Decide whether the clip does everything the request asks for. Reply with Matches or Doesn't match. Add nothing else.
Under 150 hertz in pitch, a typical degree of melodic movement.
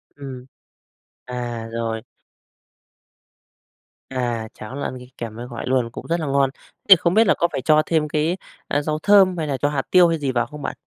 Matches